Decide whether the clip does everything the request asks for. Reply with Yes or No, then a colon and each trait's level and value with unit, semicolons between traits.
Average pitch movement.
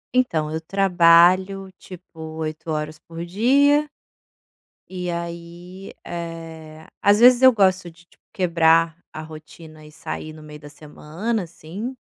Yes: average, 3.2 semitones